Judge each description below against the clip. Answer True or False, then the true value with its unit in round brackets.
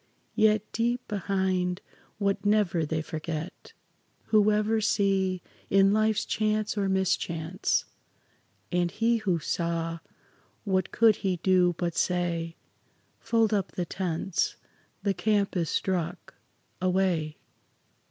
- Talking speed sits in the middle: False (115 wpm)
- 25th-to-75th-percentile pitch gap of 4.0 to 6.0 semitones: False (3.3 semitones)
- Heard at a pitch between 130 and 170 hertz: False (190 Hz)